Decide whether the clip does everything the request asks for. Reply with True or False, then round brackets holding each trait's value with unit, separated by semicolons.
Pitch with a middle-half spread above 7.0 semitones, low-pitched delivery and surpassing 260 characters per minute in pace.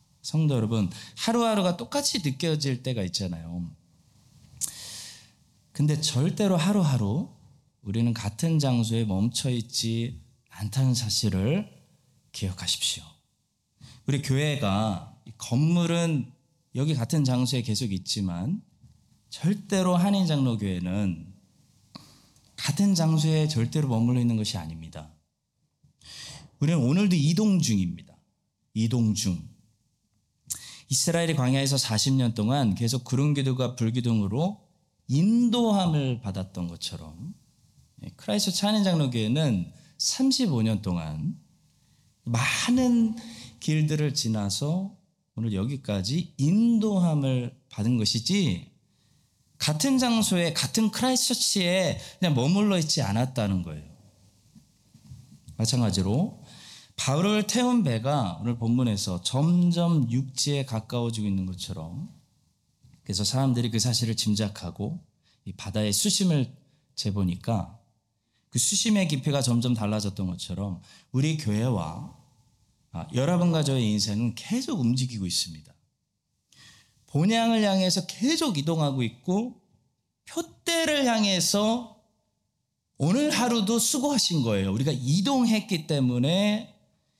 False (7.9 semitones; 130 Hz; 250 characters per minute)